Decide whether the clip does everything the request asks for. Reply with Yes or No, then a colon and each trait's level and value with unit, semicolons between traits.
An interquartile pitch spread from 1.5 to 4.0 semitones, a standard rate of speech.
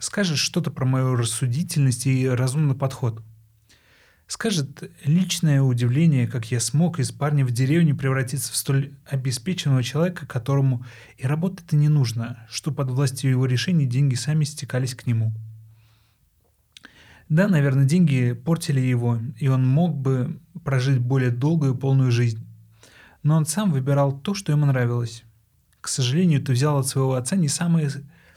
Yes: average, 3.3 semitones; average, 150 wpm